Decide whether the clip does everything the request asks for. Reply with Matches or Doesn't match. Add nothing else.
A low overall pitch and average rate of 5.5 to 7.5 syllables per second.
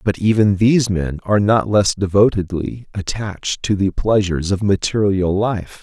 Doesn't match